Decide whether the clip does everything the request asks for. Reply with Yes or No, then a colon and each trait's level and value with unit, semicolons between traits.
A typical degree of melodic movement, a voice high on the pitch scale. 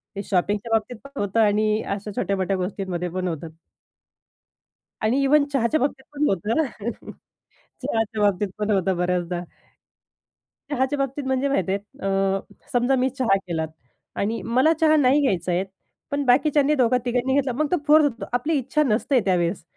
No: wide, 5.9 semitones; high, 225 Hz